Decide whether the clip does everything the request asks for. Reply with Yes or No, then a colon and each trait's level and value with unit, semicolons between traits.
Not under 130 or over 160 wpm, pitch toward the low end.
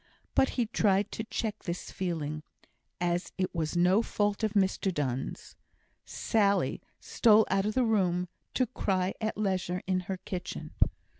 No: average, 150 wpm; high, 190 Hz